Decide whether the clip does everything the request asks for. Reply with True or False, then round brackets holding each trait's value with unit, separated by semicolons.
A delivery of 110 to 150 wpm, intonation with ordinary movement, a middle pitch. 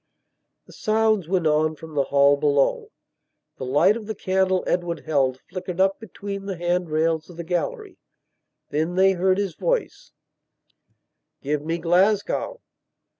True (145 wpm; 3.7 semitones; 175 Hz)